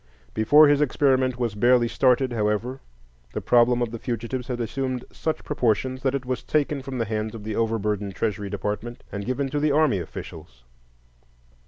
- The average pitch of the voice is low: Yes, low, 120 Hz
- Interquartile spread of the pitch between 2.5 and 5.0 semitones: Yes, average, 3.5 semitones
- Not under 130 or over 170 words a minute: No, average, 180 wpm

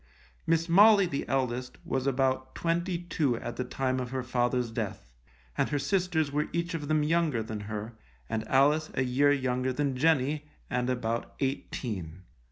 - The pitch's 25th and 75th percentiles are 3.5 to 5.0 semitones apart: Yes, average, 3.9 semitones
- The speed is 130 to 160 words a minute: No, average, 170 wpm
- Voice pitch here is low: Yes, low, 130 Hz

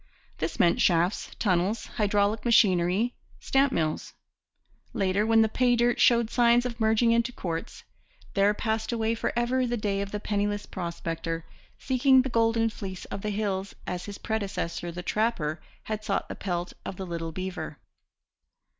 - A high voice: Yes, high, 210 Hz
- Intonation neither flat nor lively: Yes, average, 4.1 semitones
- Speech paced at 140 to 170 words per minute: Yes, average, 160 wpm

